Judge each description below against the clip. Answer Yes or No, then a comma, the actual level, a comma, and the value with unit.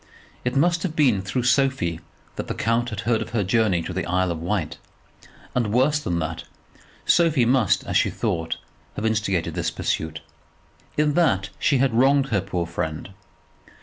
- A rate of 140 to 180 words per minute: Yes, average, 170 wpm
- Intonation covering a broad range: Yes, wide, 7.0 semitones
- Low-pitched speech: Yes, low, 110 Hz